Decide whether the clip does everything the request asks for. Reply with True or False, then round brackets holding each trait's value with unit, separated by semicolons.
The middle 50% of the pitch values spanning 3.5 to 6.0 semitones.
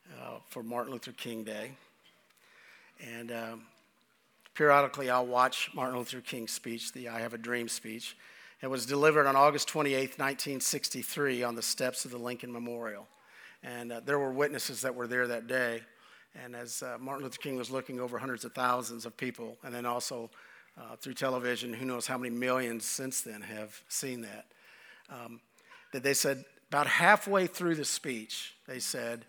False (2.4 semitones)